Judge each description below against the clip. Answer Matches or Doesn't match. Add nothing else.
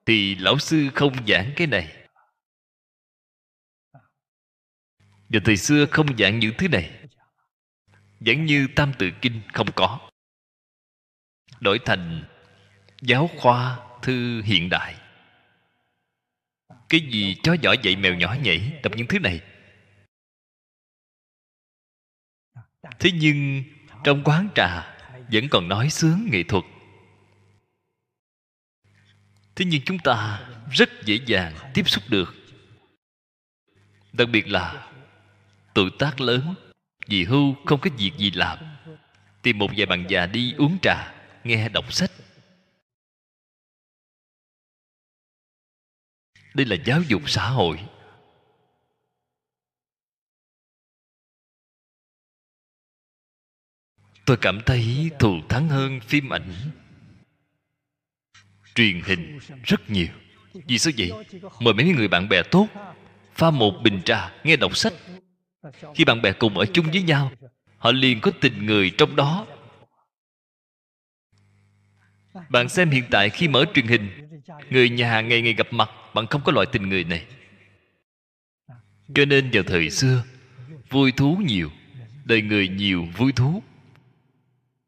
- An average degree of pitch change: Doesn't match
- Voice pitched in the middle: Doesn't match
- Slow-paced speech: Matches